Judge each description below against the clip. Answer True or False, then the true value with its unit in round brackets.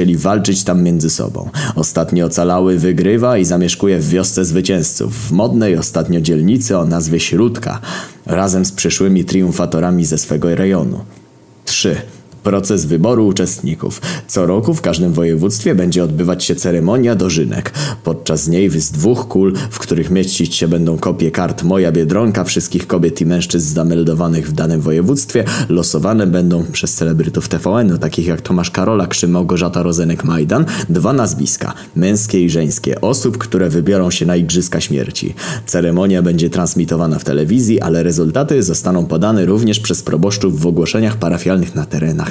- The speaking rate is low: False (150 wpm)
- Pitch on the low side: True (85 Hz)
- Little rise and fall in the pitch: True (1.8 semitones)